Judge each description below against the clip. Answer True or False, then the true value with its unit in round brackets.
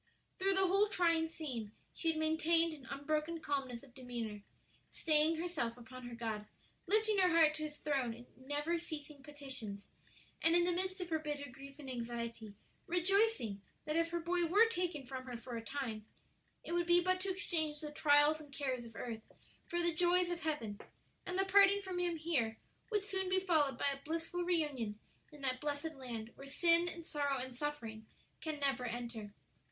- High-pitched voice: True (300 Hz)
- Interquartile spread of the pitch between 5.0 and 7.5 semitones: True (5.3 semitones)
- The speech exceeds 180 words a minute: True (190 wpm)